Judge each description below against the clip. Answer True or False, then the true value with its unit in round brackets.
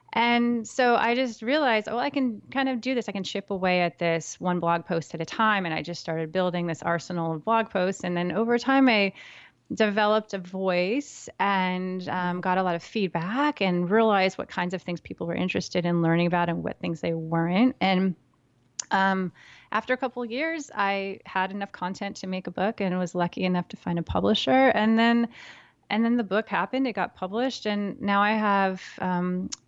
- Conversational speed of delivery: False (210 wpm)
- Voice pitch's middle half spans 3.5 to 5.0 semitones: True (4.1 semitones)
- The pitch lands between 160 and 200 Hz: True (190 Hz)